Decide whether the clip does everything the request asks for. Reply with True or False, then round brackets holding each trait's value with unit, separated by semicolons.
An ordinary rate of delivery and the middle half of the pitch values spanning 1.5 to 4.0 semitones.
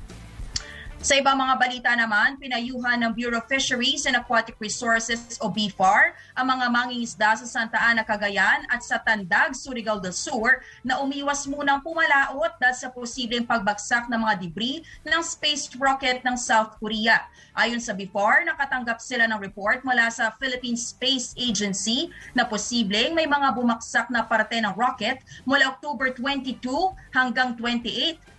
True (150 wpm; 2.8 semitones)